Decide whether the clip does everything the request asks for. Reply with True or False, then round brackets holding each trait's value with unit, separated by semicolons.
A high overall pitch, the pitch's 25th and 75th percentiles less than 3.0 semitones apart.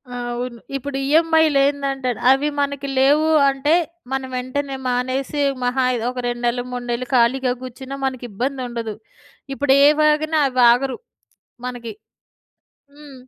True (265 Hz; 2.4 semitones)